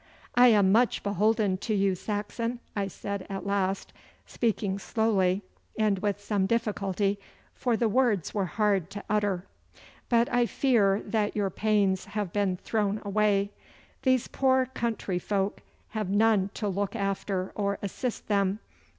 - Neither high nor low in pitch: No, high, 205 Hz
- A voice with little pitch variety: Yes, narrow, 2.0 semitones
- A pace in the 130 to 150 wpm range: Yes, average, 145 wpm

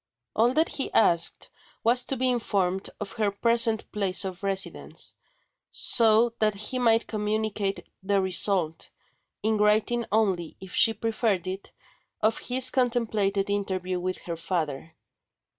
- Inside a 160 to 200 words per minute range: No, slow, 135 wpm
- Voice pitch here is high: Yes, high, 210 Hz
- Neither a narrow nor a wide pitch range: Yes, average, 3.1 semitones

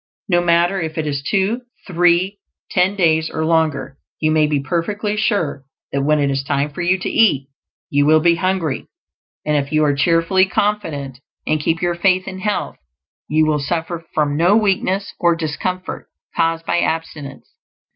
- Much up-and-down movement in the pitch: No, average, 3.6 semitones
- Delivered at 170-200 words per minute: Yes, average, 175 wpm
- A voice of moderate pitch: Yes, medium, 165 Hz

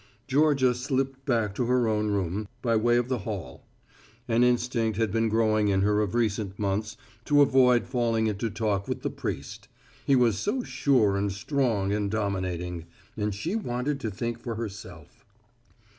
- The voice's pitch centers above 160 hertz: No, low, 115 Hz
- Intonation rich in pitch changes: No, average, 3.4 semitones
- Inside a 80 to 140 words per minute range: No, average, 170 wpm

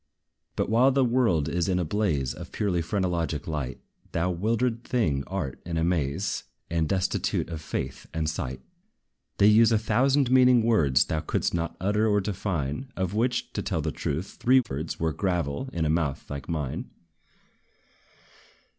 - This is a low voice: Yes, very low, 90 Hz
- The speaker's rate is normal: Yes, average, 165 wpm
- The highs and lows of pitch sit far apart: Yes, wide, 6.1 semitones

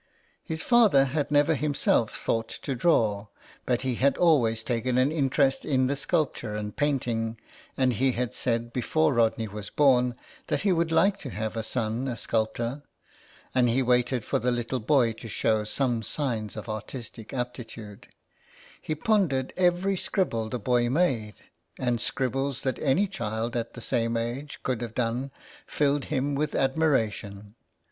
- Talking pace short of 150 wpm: No, average, 160 wpm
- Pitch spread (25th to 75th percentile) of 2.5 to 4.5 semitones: Yes, average, 3.8 semitones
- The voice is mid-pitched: No, low, 125 Hz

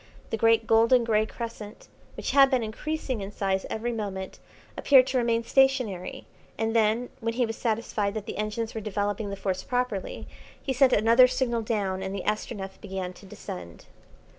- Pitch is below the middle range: No, high, 225 Hz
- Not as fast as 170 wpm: No, average, 175 wpm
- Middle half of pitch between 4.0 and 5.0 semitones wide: No, average, 3.0 semitones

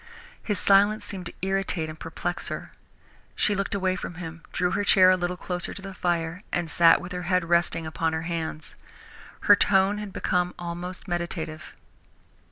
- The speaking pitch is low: No, medium, 180 Hz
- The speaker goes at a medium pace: Yes, average, 175 wpm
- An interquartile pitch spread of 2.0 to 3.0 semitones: Yes, narrow, 2.4 semitones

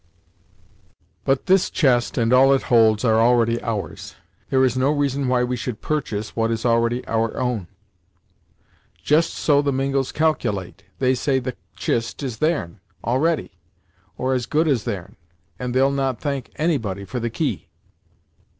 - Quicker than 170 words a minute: No, average, 155 wpm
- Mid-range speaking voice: No, low, 125 Hz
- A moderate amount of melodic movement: Yes, average, 3.2 semitones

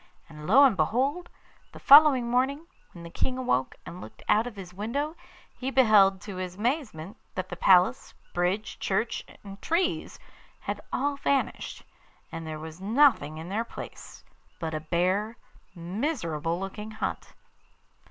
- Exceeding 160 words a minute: No, average, 150 wpm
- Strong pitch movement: Yes, wide, 6.6 semitones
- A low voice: No, high, 205 Hz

